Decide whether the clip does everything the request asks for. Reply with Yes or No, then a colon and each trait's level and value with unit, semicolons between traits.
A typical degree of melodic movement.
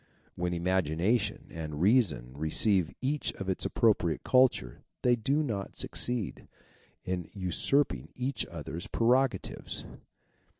No: wide, 6.4 semitones